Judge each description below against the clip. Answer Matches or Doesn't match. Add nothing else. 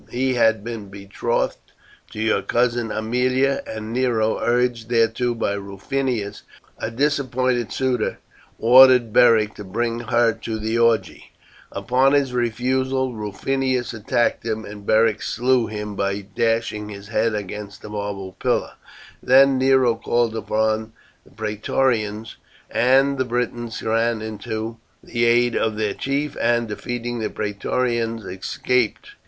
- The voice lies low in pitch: Matches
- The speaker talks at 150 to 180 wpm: Doesn't match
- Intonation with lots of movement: Doesn't match